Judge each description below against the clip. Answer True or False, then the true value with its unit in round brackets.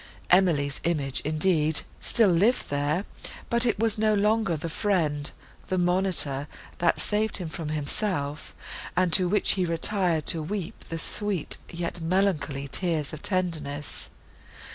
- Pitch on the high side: False (170 Hz)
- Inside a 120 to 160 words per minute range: True (140 wpm)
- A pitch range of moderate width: True (4.3 semitones)